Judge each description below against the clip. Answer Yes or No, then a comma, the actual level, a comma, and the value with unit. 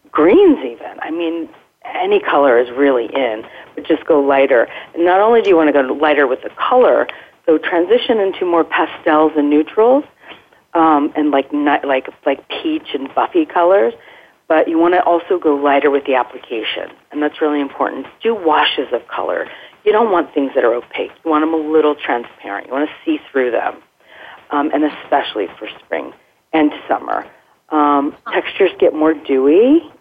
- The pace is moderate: Yes, average, 180 wpm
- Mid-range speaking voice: Yes, medium, 160 Hz